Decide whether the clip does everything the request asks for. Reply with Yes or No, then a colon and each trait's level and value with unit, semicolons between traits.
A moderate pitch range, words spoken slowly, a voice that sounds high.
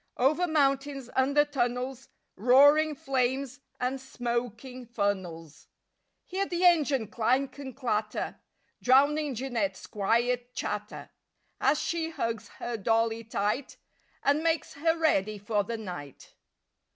Yes: average, 4.0 semitones; slow, 115 wpm; very high, 250 Hz